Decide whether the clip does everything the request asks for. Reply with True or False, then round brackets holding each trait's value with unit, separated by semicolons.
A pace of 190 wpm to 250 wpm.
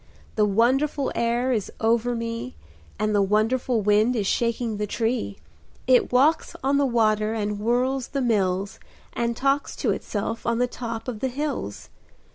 False (160 wpm)